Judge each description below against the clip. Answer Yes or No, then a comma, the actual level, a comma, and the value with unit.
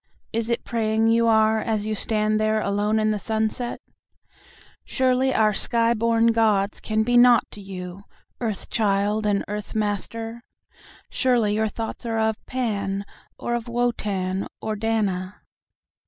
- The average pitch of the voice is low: No, high, 220 Hz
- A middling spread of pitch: No, narrow, 1.9 semitones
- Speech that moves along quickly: No, average, 140 wpm